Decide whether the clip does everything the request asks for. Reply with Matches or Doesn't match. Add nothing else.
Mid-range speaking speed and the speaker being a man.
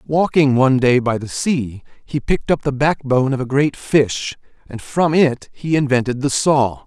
Matches